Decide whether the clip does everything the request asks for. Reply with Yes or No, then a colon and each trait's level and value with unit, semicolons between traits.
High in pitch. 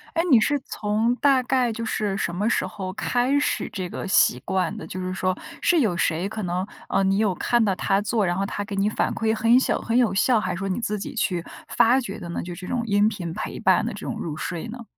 Yes: high, 205 Hz